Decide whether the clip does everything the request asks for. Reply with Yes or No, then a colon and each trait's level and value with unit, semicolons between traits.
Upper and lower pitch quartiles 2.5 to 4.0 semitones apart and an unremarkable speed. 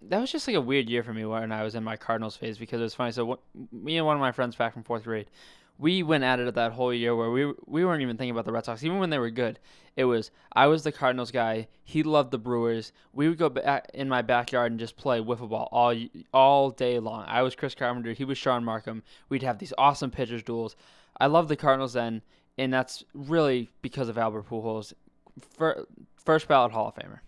No: average, 3.1 semitones; fast, 250 wpm